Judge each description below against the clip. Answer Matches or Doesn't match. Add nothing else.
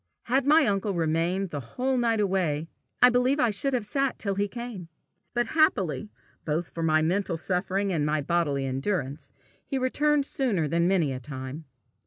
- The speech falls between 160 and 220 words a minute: Matches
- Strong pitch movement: Matches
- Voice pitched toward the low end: Doesn't match